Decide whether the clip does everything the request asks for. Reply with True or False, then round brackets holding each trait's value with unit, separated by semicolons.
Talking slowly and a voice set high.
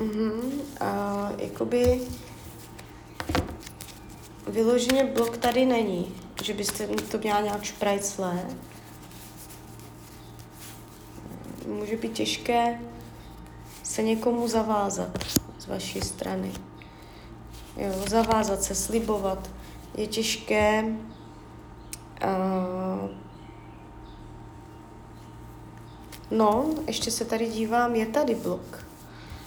True (80 wpm; 220 Hz)